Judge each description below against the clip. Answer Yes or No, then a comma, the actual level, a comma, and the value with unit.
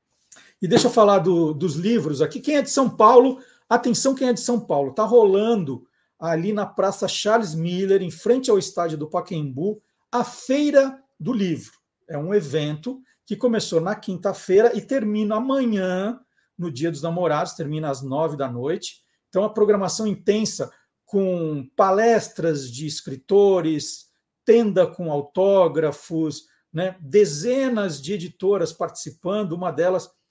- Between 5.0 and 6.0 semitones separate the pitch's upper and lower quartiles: Yes, average, 5.3 semitones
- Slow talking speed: No, average, 145 wpm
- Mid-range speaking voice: No, high, 195 Hz